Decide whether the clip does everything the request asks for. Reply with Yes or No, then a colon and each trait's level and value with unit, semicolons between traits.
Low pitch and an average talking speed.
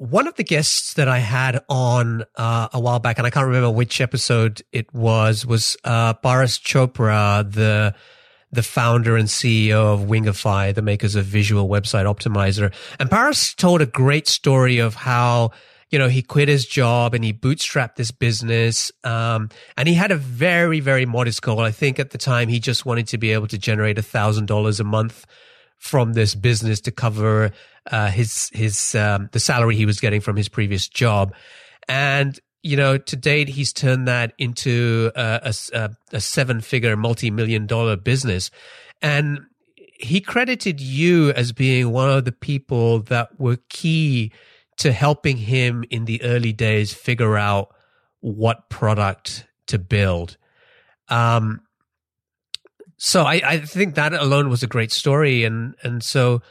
Yes: low, 120 Hz; average, 170 wpm